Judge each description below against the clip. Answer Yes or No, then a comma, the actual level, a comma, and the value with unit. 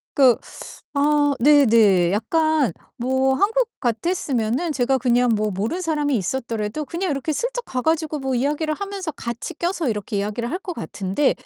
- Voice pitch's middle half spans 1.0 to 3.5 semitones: No, average, 5.3 semitones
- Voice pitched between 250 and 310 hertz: Yes, very high, 270 Hz